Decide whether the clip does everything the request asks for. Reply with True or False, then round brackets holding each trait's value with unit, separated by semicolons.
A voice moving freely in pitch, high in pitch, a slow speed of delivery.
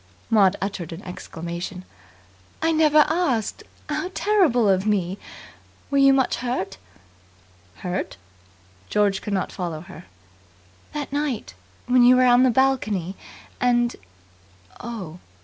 True (6.1 semitones; 220 Hz; 125 wpm)